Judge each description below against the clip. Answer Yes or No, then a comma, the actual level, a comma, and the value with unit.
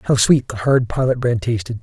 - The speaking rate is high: Yes, fast, 230 wpm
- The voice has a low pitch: Yes, low, 120 Hz